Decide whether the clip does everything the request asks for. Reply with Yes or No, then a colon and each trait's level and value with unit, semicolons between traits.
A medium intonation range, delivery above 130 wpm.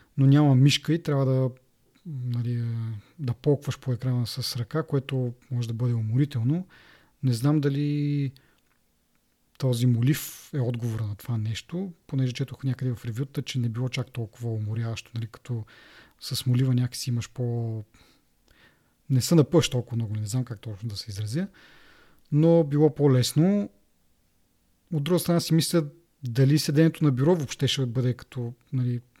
Yes: average, 3.7 semitones; average, 155 wpm